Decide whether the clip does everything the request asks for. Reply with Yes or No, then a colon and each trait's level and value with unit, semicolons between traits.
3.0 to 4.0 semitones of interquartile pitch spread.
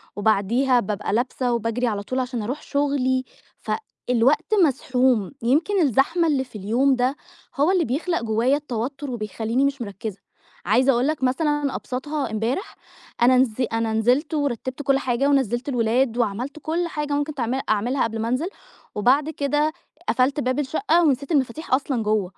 Yes: average, 3.7 semitones